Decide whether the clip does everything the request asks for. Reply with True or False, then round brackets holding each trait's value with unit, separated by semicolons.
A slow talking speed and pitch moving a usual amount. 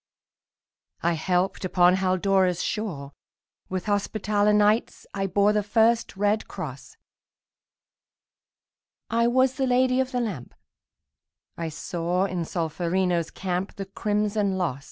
True (115 wpm; 3.1 semitones)